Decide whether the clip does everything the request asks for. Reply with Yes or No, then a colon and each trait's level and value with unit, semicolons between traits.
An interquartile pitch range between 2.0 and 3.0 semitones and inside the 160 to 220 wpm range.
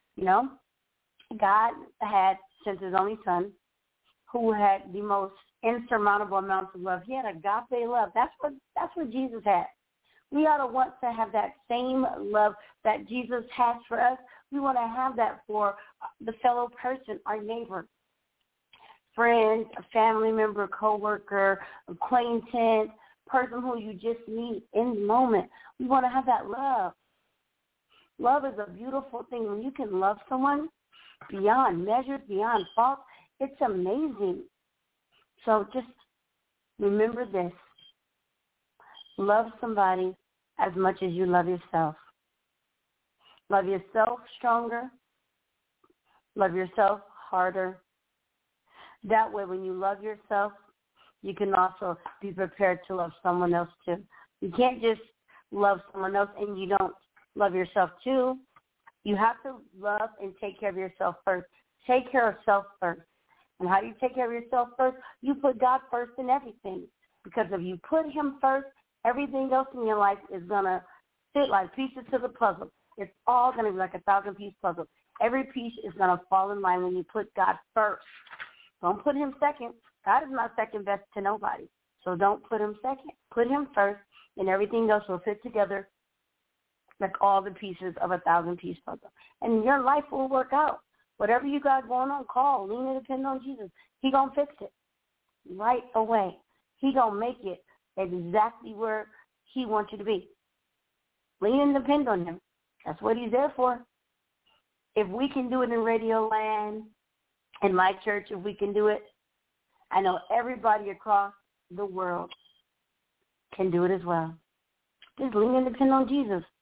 No: average, 4.4 semitones; average, 165 wpm